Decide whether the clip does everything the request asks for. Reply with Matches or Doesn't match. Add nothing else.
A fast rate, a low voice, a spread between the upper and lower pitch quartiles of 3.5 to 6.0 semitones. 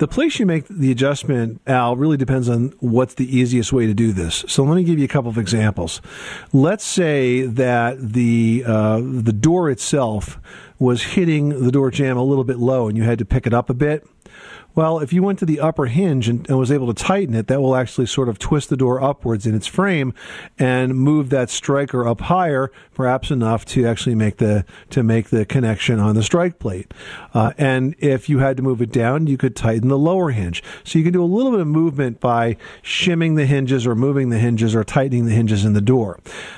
Matches